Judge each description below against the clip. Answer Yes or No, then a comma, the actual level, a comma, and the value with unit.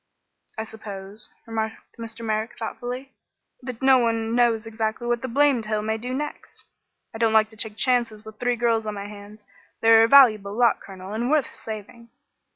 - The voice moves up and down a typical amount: No, narrow, 1.9 semitones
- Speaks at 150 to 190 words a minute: Yes, average, 185 wpm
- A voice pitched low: No, high, 225 Hz